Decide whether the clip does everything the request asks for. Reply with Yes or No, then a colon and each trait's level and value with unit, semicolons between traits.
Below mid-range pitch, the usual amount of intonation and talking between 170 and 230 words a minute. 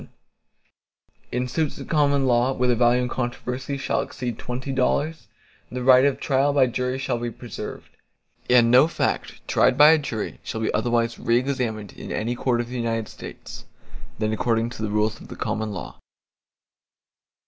No: low, 125 Hz; narrow, 2.3 semitones; average, 180 wpm